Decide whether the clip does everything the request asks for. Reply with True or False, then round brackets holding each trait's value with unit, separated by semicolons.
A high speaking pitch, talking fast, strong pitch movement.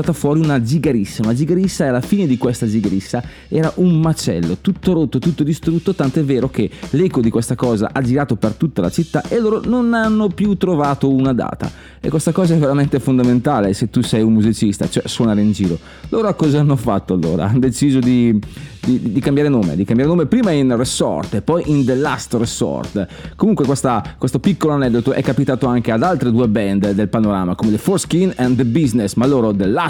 False (135 Hz; 210 wpm; 6.0 semitones)